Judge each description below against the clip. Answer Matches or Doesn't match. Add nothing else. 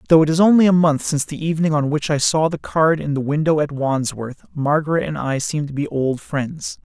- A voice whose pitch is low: Doesn't match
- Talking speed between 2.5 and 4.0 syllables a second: Doesn't match